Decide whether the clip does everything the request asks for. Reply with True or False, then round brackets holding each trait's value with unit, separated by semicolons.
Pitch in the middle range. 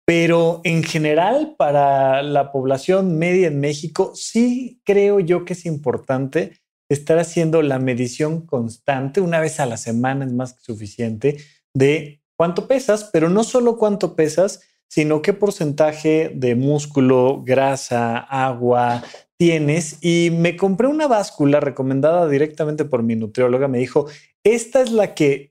True (155 Hz)